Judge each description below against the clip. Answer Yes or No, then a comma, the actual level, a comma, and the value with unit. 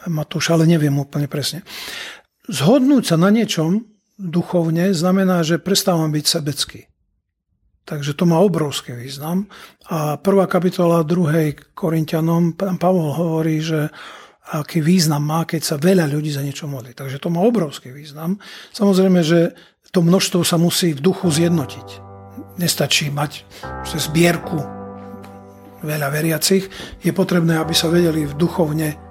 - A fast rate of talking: No, average, 135 wpm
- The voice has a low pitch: No, medium, 165 Hz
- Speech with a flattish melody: No, average, 3.2 semitones